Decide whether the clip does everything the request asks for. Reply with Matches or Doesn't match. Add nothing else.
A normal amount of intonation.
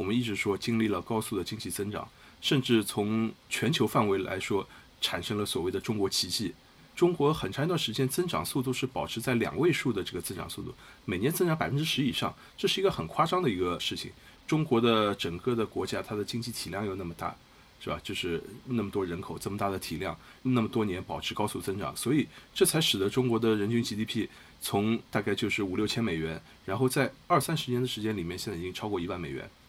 Matches